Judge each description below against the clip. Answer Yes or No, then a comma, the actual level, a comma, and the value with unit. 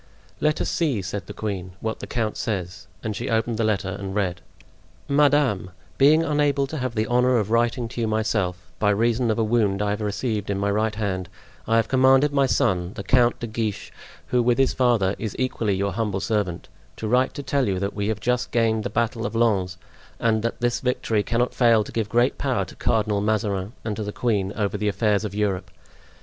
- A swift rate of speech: Yes, fast, 215 wpm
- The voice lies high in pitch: No, low, 110 Hz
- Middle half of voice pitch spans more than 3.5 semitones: No, average, 3.1 semitones